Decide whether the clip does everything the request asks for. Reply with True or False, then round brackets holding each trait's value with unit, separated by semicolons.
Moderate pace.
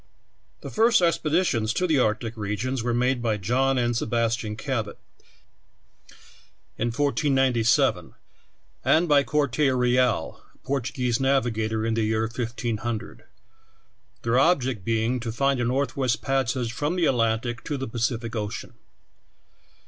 False (130 wpm)